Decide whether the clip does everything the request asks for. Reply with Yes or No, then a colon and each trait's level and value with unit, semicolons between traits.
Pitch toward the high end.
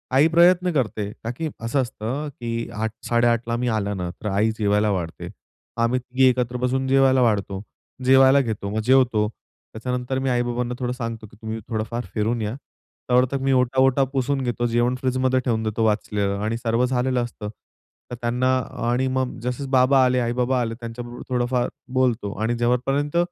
No: low, 120 Hz